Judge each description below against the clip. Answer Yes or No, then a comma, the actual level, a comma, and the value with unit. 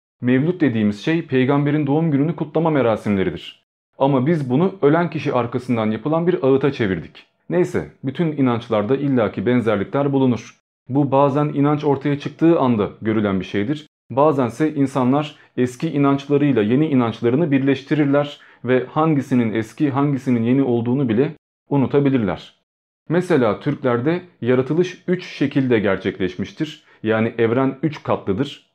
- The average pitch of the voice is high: No, medium, 140 Hz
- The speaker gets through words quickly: No, average, 120 wpm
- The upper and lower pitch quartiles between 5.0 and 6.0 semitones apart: No, average, 3.7 semitones